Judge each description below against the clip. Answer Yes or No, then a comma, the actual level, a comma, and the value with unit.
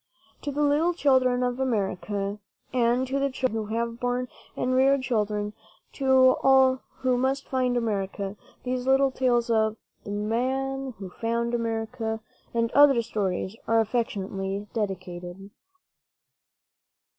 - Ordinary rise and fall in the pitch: Yes, average, 3.7 semitones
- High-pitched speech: Yes, high, 235 Hz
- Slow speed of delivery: Yes, slow, 130 wpm